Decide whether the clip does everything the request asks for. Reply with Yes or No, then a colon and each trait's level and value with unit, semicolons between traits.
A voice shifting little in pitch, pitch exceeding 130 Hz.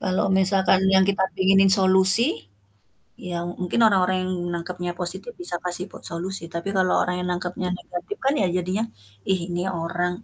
Yes: narrow, 1.4 semitones; medium, 185 Hz